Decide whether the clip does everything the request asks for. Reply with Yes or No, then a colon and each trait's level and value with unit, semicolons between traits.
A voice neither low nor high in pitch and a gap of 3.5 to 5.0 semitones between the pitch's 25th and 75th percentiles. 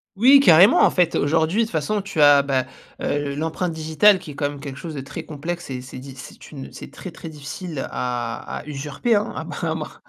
Yes: medium, 155 Hz; average, 4.2 semitones